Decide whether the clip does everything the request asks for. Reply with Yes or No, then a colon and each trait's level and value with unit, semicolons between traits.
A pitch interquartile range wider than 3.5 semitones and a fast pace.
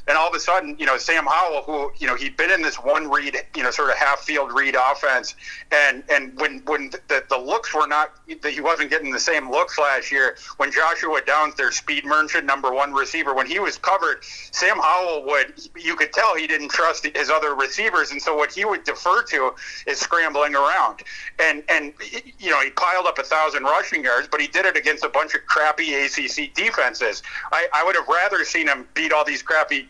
Yes: average, 4.2 semitones; fast, 220 wpm